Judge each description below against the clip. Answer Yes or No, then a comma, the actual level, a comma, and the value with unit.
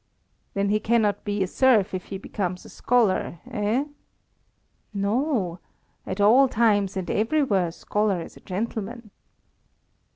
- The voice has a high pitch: Yes, high, 205 Hz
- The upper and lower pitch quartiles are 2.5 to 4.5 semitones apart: Yes, average, 3.2 semitones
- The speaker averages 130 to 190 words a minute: Yes, slow, 135 wpm